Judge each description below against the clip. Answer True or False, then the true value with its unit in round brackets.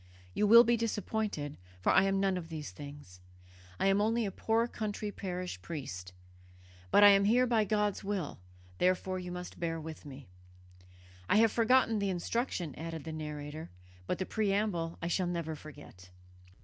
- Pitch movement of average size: True (5.0 semitones)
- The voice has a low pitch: False (185 Hz)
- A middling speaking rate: True (170 wpm)